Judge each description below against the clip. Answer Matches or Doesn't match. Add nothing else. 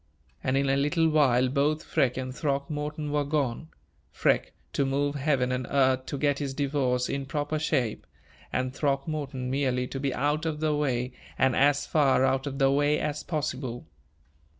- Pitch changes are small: Matches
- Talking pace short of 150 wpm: Doesn't match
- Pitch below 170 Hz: Matches